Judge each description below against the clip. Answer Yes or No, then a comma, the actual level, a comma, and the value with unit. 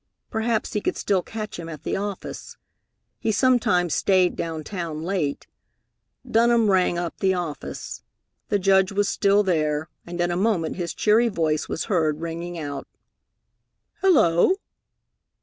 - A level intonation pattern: No, average, 4.0 semitones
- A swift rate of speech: No, average, 145 wpm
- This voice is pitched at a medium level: Yes, medium, 180 Hz